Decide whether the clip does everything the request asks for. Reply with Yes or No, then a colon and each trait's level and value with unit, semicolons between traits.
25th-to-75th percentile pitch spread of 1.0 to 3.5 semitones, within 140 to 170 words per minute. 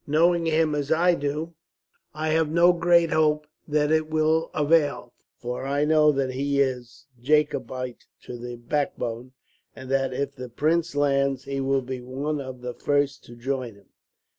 Yes: average, 3.2 semitones; average, 165 wpm